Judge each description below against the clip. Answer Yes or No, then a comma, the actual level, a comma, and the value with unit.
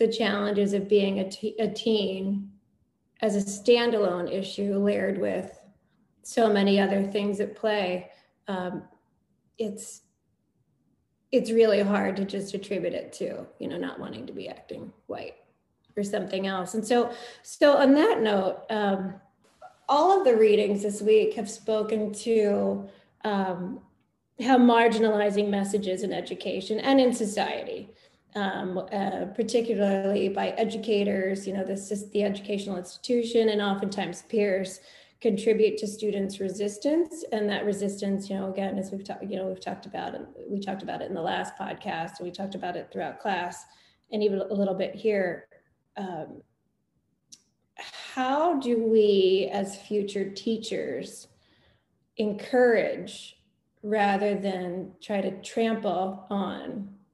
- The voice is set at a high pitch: Yes, high, 205 Hz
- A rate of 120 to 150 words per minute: Yes, average, 140 wpm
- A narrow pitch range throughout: Yes, narrow, 2.3 semitones